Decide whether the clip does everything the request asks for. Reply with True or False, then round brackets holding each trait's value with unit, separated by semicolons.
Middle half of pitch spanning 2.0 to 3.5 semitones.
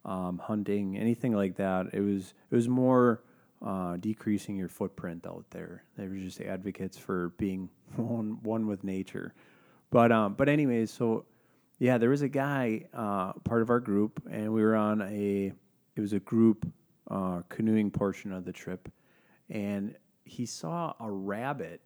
True (3.2 semitones)